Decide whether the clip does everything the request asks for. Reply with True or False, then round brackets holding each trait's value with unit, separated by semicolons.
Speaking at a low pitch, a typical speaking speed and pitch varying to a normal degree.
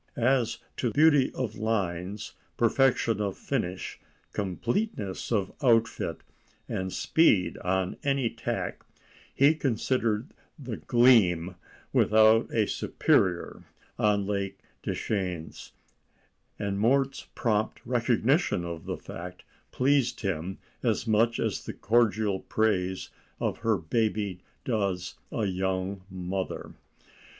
False (105 Hz; 105 wpm; 4.1 semitones)